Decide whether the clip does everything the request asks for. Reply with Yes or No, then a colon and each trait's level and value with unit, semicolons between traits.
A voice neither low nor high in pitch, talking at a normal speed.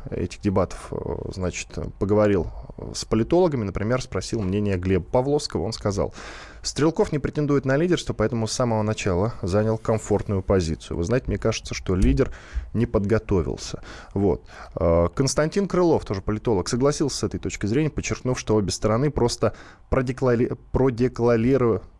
No: low, 110 Hz; average, 135 wpm